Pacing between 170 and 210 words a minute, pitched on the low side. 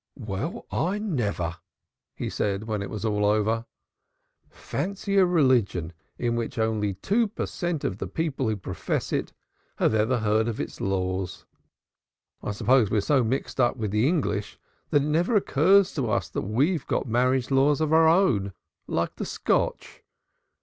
No: average, 160 wpm; low, 120 Hz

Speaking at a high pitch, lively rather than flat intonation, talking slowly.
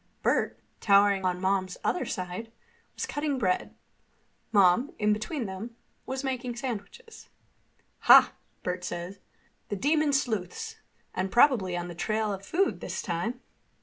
Yes: high, 215 Hz; wide, 5.8 semitones; slow, 125 wpm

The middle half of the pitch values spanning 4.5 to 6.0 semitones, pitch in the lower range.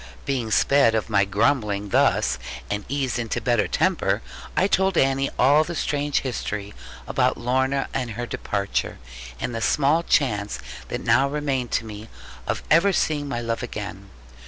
Yes: average, 5.0 semitones; low, 125 Hz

